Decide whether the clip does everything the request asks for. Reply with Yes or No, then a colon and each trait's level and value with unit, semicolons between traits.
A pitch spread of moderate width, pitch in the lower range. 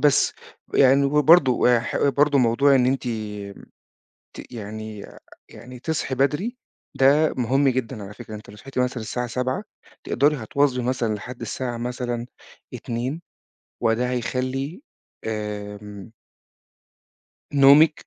Yes: average, 3.2 semitones; low, 125 Hz